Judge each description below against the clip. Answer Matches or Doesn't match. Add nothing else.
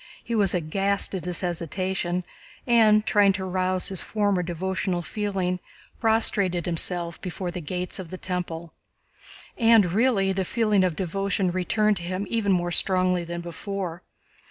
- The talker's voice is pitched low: Doesn't match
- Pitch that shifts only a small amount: Matches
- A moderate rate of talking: Matches